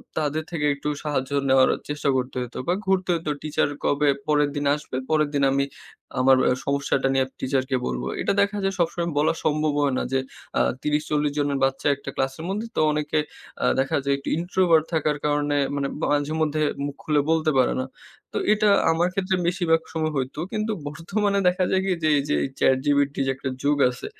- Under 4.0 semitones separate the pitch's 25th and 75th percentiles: Yes, average, 2.8 semitones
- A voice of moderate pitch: Yes, medium, 150 Hz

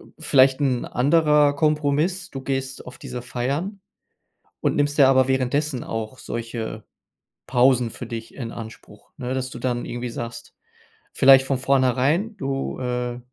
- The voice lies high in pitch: No, low, 130 Hz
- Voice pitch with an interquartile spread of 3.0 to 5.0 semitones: No, narrow, 2.6 semitones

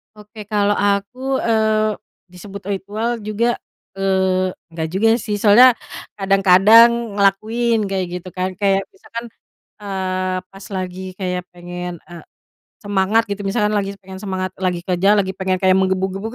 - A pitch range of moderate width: No, narrow, 2.3 semitones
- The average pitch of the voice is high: Yes, high, 195 Hz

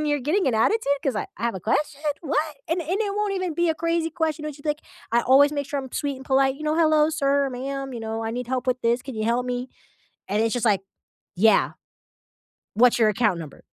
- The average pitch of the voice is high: Yes, very high, 275 Hz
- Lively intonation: No, average, 4.5 semitones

